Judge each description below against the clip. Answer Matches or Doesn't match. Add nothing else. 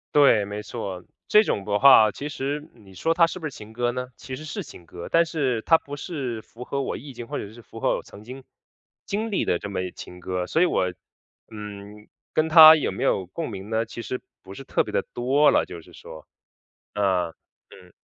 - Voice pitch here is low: Matches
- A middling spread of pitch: Doesn't match